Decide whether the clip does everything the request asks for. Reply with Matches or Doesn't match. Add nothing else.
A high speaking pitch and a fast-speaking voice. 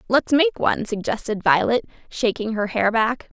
Doesn't match